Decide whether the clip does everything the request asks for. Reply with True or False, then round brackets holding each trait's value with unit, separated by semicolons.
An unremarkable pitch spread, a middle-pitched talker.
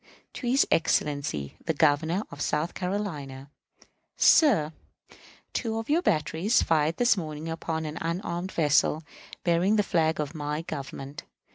True (4.1 semitones; 160 Hz)